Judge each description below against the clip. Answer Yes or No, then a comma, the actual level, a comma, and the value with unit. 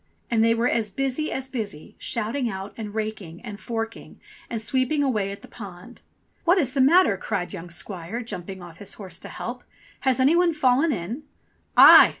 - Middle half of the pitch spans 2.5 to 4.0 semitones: No, average, 4.9 semitones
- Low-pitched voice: No, high, 225 Hz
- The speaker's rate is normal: Yes, average, 190 wpm